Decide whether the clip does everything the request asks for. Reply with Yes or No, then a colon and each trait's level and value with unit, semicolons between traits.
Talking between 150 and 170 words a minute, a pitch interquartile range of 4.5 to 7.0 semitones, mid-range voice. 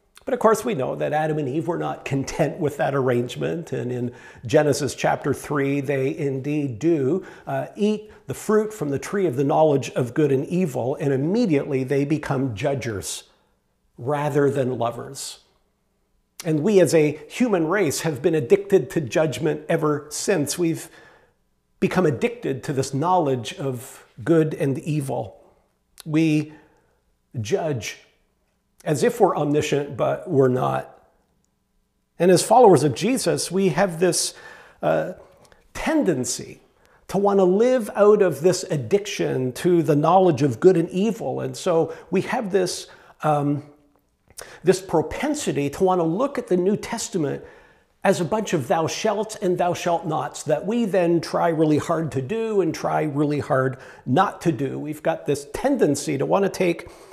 Yes: average, 160 wpm; average, 4.9 semitones; medium, 160 Hz